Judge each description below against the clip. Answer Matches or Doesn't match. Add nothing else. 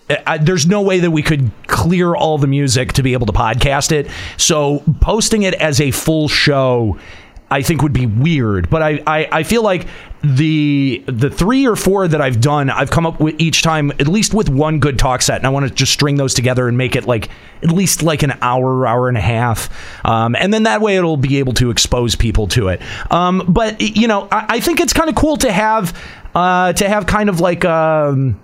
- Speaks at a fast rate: Matches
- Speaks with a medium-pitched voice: Matches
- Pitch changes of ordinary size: Doesn't match